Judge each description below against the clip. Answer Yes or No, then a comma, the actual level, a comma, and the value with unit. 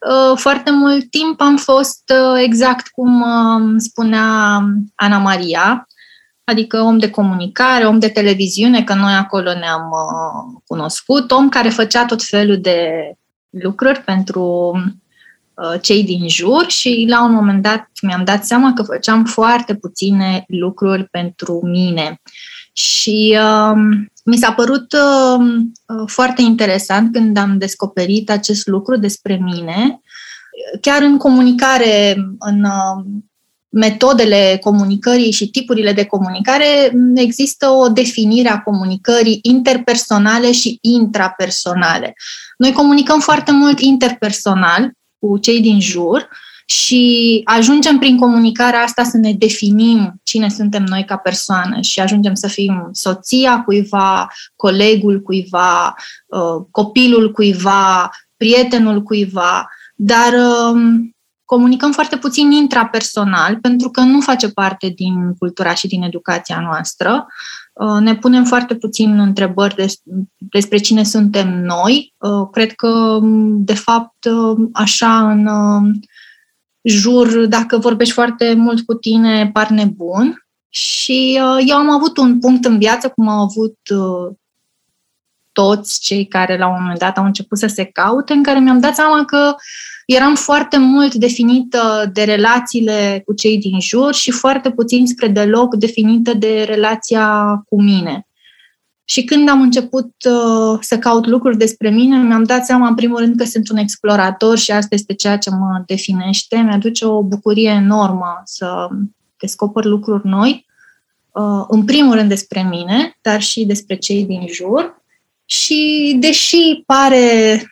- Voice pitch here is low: No, high, 220 Hz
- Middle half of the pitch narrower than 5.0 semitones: Yes, average, 3.7 semitones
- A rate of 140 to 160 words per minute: No, average, 130 wpm